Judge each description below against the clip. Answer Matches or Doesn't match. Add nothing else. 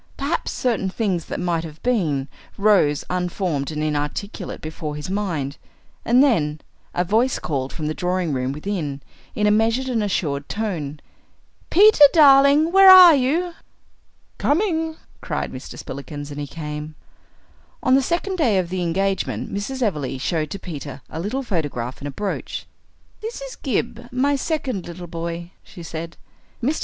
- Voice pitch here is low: Doesn't match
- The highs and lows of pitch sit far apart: Matches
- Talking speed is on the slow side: Doesn't match